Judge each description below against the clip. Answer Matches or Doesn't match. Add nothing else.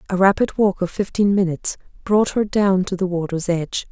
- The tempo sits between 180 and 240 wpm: Matches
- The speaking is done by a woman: Matches